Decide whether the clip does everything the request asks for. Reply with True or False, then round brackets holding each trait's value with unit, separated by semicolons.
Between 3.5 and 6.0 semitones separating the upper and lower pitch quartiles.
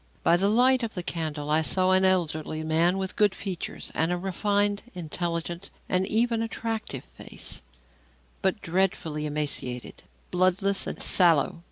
True (3.8 semitones)